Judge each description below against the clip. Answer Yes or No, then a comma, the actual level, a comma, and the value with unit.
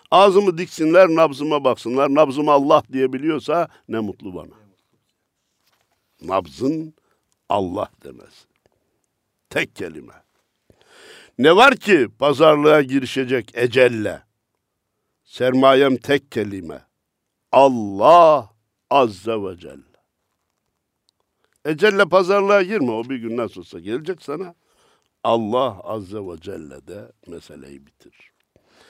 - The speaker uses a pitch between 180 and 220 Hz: No, low, 135 Hz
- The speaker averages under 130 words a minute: Yes, slow, 95 wpm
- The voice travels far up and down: Yes, wide, 5.7 semitones